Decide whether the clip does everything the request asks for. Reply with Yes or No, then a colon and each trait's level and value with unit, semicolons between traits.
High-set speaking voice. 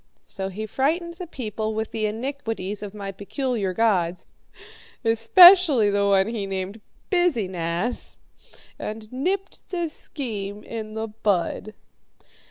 Yes: high, 220 Hz